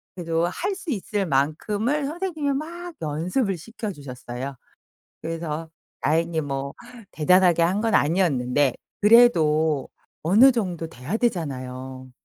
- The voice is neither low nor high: Yes, medium, 170 Hz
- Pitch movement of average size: No, wide, 7.5 semitones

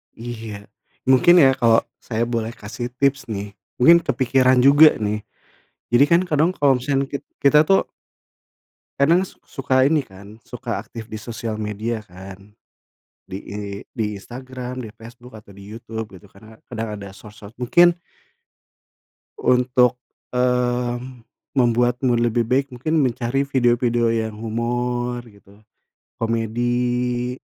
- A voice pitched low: Yes, low, 120 Hz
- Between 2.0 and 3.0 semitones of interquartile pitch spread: Yes, narrow, 2.6 semitones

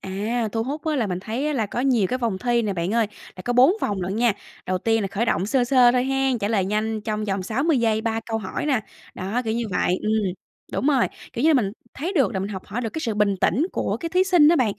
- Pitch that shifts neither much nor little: Yes, average, 4.1 semitones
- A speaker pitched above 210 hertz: Yes, high, 225 Hz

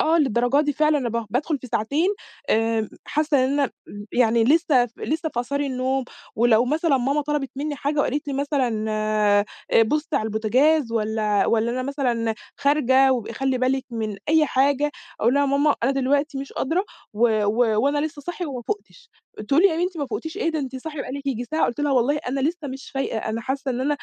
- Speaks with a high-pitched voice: Yes, very high, 270 Hz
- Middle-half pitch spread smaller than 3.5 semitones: No, average, 3.8 semitones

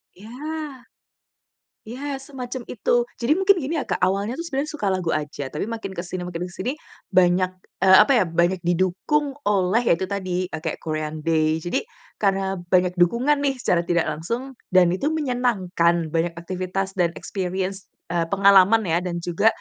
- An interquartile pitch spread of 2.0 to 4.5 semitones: No, average, 5.1 semitones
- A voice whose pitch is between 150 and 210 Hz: Yes, high, 190 Hz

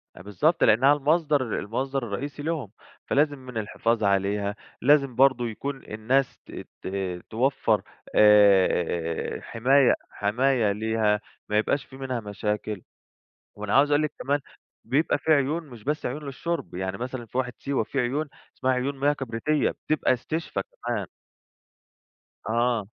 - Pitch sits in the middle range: No, low, 125 Hz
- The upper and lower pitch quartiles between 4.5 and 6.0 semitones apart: Yes, average, 5.0 semitones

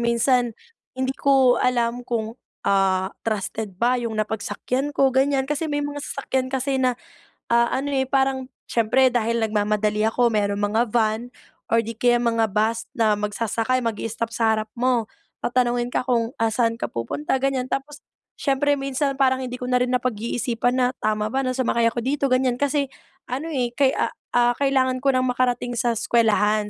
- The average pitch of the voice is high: Yes, high, 245 Hz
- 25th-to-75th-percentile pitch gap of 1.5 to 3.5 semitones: Yes, average, 2.9 semitones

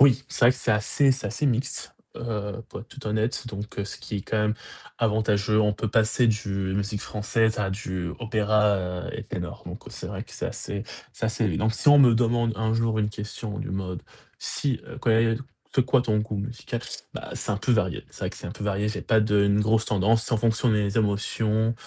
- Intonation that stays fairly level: Yes, narrow, 1.8 semitones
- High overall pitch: No, low, 110 Hz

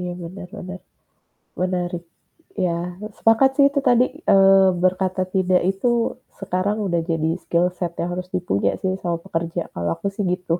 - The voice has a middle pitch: Yes, medium, 180 Hz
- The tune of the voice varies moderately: No, narrow, 1.9 semitones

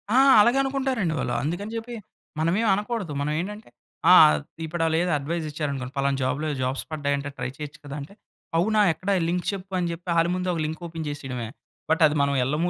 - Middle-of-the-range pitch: Yes, medium, 160 Hz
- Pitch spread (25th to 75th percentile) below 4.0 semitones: No, average, 4.6 semitones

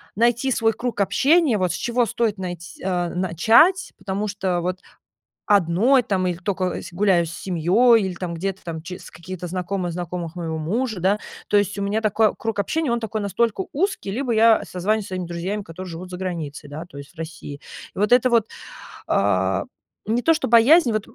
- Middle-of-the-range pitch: No, high, 195 Hz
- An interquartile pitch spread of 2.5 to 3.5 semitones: No, average, 4.3 semitones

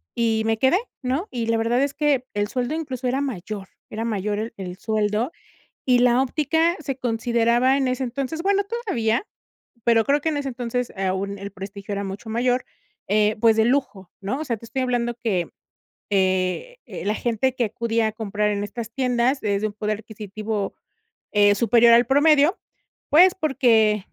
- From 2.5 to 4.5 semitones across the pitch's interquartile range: Yes, average, 3.9 semitones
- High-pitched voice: Yes, high, 235 Hz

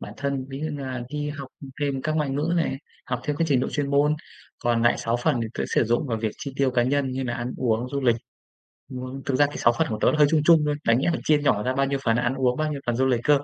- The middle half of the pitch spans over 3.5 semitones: No, average, 3.1 semitones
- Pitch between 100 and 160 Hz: Yes, low, 135 Hz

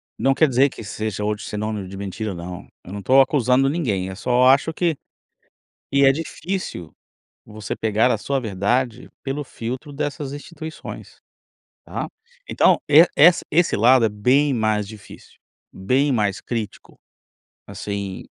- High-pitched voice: No, low, 125 Hz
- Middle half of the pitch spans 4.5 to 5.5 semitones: Yes, average, 5.2 semitones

